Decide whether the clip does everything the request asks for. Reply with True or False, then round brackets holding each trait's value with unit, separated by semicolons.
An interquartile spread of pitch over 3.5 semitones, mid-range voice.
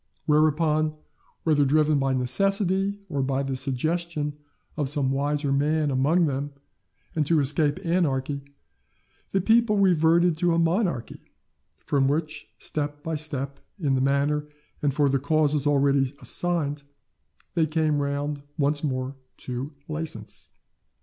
False (2.6 semitones; 150 Hz)